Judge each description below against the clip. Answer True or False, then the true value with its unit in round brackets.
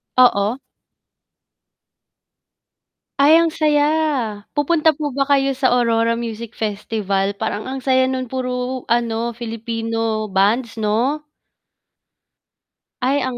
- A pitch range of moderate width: True (3.1 semitones)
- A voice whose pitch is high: True (240 Hz)